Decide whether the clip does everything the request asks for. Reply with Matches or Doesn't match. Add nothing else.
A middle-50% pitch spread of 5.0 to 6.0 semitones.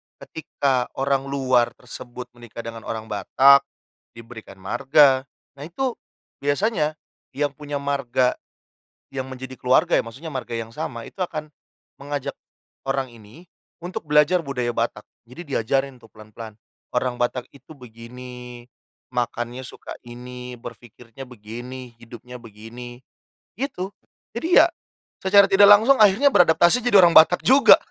Doesn't match